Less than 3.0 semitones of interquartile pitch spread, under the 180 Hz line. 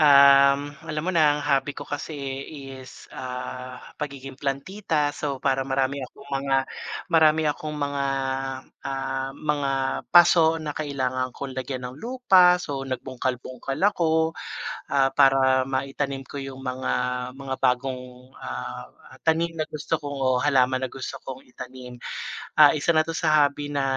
Yes: narrow, 2.5 semitones; medium, 140 Hz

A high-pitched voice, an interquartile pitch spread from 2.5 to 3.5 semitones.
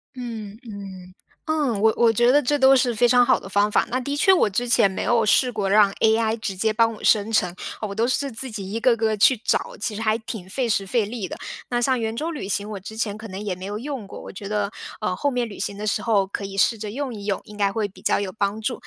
Yes: high, 220 Hz; average, 3.1 semitones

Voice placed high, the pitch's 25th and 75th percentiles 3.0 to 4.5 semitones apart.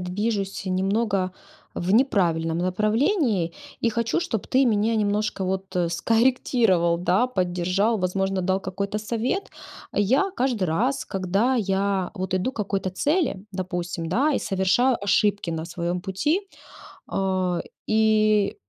Yes: high, 200 Hz; average, 3.8 semitones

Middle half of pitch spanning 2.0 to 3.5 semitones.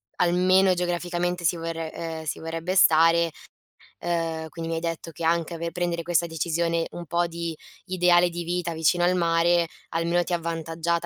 No: narrow, 1.0 semitones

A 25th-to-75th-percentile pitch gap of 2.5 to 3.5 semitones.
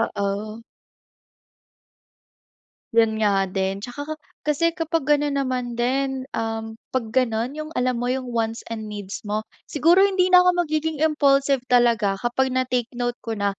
No: average, 4.6 semitones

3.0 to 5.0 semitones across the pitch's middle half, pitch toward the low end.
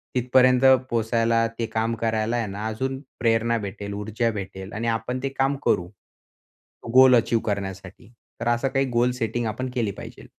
No: narrow, 2.5 semitones; low, 115 Hz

